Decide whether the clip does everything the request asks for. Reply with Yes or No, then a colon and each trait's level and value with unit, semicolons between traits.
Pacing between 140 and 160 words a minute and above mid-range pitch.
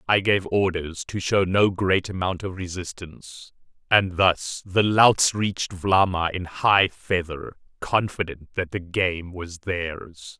No: average, 145 wpm; very low, 90 Hz